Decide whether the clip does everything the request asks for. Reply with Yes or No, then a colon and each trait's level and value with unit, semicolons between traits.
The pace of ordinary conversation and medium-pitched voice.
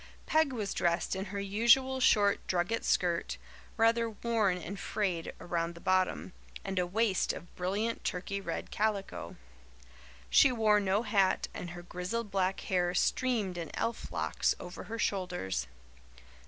No: average, 145 wpm; high, 195 Hz